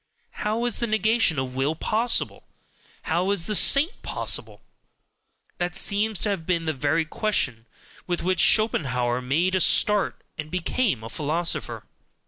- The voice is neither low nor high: Yes, medium, 175 Hz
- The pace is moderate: Yes, average, 145 wpm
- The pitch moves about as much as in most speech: No, wide, 6.1 semitones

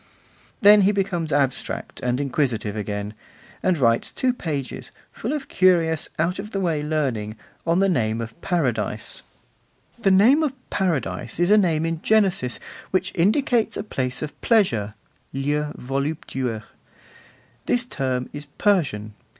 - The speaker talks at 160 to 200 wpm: No, average, 140 wpm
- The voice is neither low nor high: Yes, medium, 155 Hz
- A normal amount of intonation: No, wide, 7.4 semitones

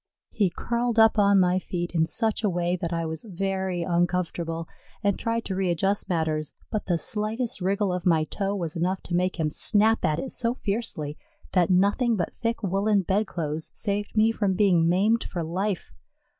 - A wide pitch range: No, average, 3.6 semitones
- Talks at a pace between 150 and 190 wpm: Yes, average, 185 wpm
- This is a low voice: No, high, 190 Hz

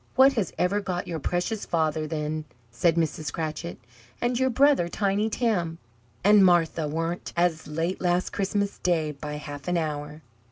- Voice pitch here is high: No, medium, 170 Hz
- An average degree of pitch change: Yes, average, 4.1 semitones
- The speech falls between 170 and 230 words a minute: No, average, 160 wpm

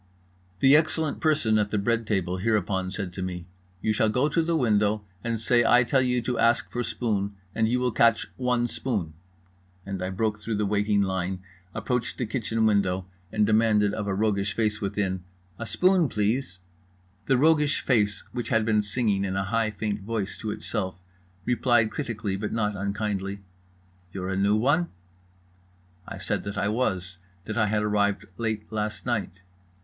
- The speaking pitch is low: Yes, low, 105 Hz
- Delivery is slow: No, average, 175 wpm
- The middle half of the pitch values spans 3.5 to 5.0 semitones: No, average, 3.1 semitones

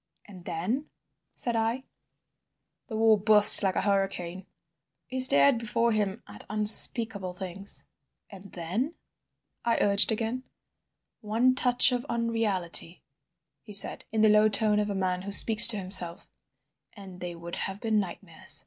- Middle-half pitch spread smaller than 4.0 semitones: Yes, average, 3.3 semitones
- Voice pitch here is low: No, high, 210 Hz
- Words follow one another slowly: No, average, 145 wpm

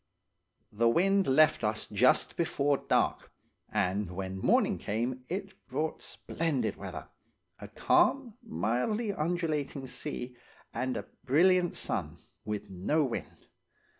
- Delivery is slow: Yes, slow, 110 wpm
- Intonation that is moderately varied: No, wide, 7.9 semitones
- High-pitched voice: No, low, 135 Hz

